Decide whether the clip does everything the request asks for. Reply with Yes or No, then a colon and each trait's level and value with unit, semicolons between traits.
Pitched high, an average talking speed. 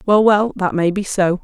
No: high, 195 Hz; fast, 250 wpm